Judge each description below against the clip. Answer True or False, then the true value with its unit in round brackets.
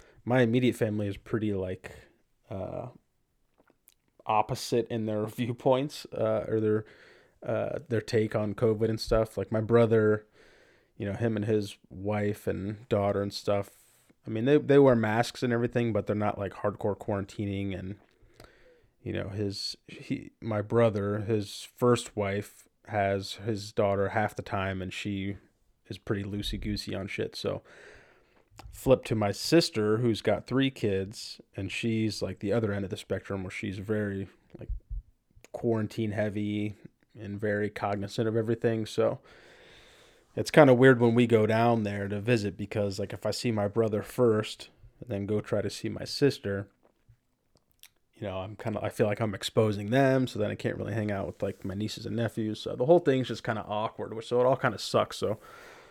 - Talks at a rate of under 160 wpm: False (175 wpm)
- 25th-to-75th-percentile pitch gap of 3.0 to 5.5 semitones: False (2.6 semitones)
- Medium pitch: False (110 Hz)